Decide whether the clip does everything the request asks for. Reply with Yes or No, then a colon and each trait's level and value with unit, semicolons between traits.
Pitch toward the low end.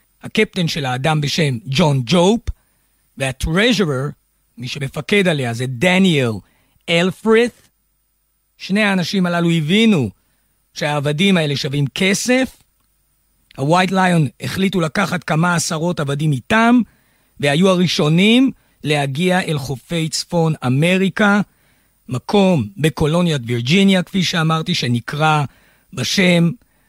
No: medium, 165 Hz